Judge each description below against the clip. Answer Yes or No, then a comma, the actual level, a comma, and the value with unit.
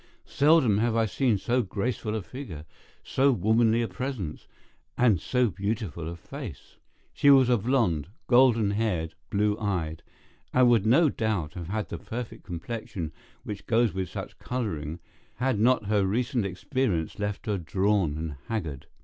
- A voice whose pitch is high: No, low, 110 Hz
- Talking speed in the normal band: Yes, average, 155 wpm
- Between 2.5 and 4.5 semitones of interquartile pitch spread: No, average, 5.1 semitones